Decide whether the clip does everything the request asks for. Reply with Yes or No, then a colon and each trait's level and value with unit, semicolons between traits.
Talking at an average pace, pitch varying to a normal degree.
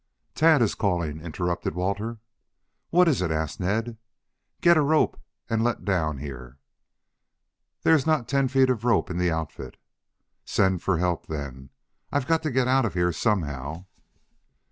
No: average, 160 wpm; wide, 8.1 semitones